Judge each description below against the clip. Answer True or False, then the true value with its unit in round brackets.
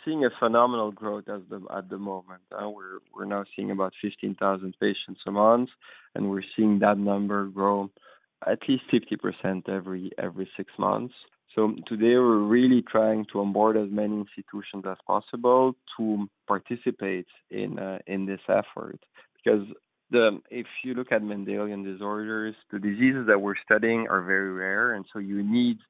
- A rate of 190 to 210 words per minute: False (165 wpm)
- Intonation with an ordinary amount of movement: False (2.2 semitones)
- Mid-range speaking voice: False (105 Hz)